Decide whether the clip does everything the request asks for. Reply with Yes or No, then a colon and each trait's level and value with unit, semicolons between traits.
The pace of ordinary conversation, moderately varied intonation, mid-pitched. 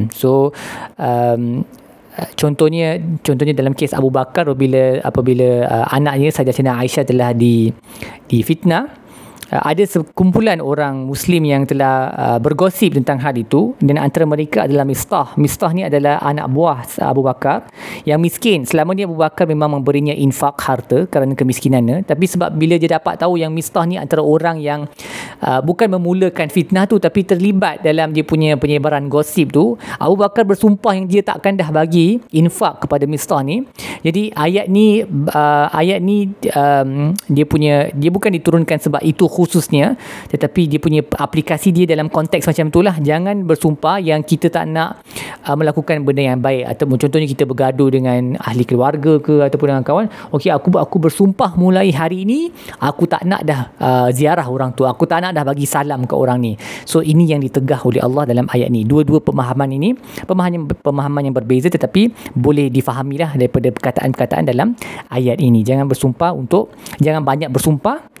No: fast, 170 wpm; average, 4.0 semitones; medium, 150 Hz